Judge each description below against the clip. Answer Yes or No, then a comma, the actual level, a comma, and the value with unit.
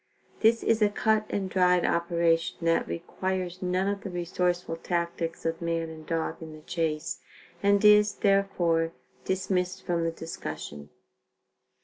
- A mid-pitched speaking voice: Yes, medium, 175 Hz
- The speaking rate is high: No, average, 140 wpm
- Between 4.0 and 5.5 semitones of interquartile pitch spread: No, average, 2.7 semitones